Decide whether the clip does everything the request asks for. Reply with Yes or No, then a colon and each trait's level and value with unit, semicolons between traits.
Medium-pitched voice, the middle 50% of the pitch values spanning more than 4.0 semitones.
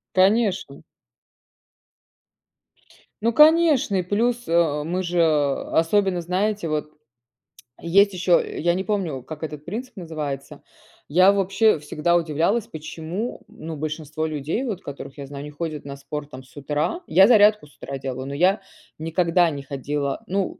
Yes: medium, 165 Hz; average, 4.8 semitones